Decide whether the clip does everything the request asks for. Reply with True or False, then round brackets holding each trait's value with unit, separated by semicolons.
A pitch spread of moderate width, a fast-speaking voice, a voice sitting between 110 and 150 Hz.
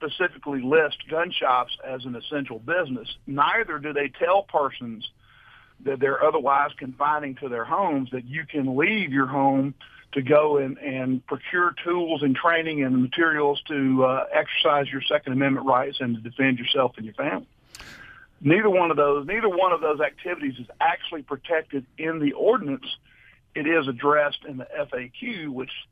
False (3.1 semitones; 165 wpm; 140 Hz)